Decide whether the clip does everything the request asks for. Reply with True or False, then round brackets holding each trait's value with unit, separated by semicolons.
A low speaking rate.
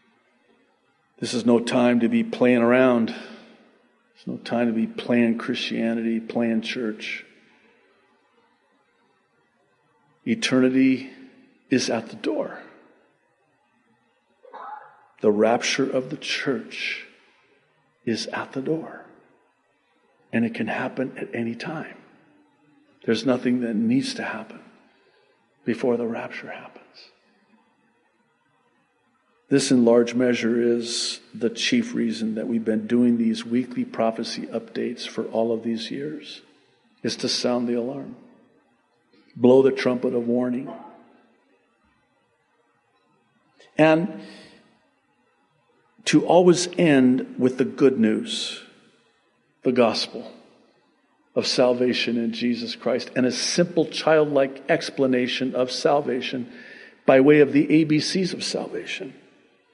True (110 wpm)